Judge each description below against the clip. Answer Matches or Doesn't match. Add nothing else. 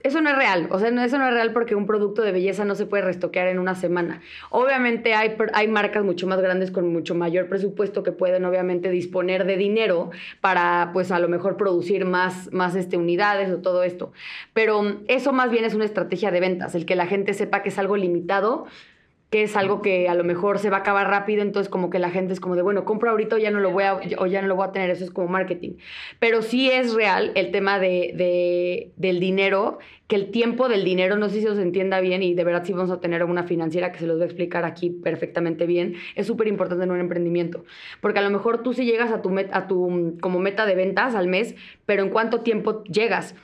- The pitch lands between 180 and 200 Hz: Matches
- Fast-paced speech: Matches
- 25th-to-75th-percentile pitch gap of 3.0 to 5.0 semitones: Doesn't match